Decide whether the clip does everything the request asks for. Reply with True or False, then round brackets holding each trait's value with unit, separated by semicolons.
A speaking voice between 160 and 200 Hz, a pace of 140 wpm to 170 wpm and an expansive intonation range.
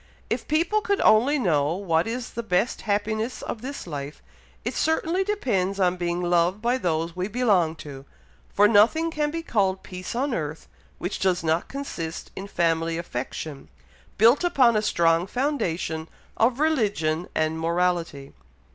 True (190 Hz; 155 wpm; 6.8 semitones)